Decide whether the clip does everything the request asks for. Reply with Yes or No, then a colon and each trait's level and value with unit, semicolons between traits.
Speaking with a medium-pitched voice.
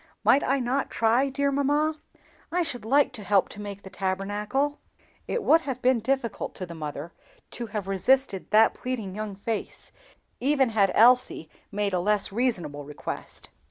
No: high, 225 Hz